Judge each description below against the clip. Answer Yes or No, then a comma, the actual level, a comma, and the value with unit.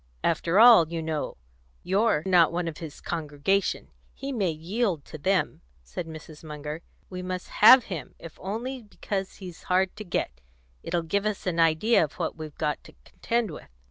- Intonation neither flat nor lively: Yes, average, 4.1 semitones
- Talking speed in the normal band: Yes, average, 175 wpm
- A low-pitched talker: No, medium, 175 Hz